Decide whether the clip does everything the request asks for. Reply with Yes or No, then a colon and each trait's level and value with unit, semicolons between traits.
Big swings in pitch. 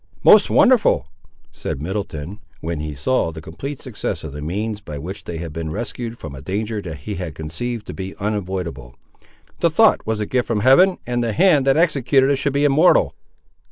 Yes: wide, 8.0 semitones